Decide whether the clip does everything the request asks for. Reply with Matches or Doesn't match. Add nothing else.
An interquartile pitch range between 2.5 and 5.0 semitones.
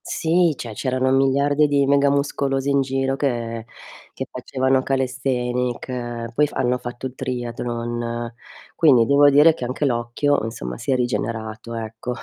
Matches